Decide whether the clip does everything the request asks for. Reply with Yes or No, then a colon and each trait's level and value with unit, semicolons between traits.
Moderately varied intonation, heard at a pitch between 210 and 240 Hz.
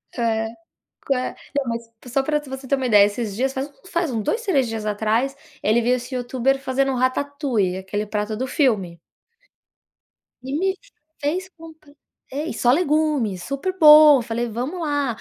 No: average, 4.3 semitones; very high, 260 Hz